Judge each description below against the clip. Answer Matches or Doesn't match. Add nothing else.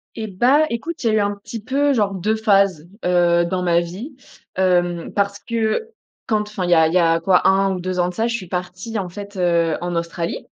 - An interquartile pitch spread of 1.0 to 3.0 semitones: Doesn't match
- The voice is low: Doesn't match